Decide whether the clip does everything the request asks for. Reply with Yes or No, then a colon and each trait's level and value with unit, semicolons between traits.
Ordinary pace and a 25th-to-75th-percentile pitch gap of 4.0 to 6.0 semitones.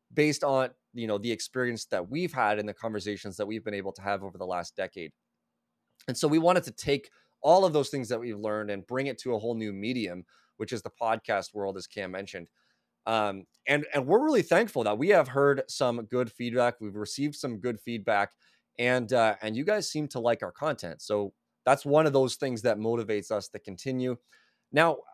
No: fast, 215 wpm; average, 4.3 semitones